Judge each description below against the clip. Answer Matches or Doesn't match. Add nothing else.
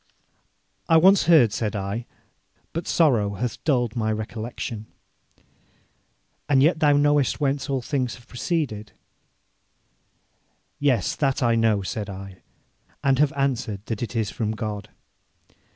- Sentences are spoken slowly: Matches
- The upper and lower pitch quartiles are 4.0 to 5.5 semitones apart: Matches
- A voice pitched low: Matches